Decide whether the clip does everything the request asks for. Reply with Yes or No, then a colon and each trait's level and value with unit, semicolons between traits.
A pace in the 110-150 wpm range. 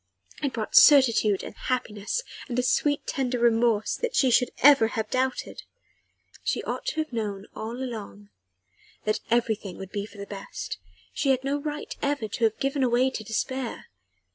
No: average, 170 wpm